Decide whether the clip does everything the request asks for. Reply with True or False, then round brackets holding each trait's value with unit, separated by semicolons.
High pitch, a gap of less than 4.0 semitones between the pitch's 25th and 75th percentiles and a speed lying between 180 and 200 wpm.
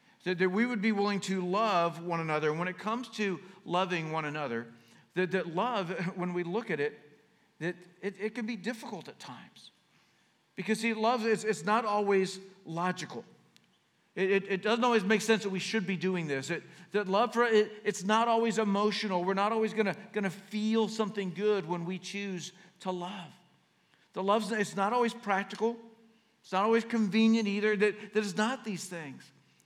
True (200 Hz; 3.2 semitones; 190 wpm)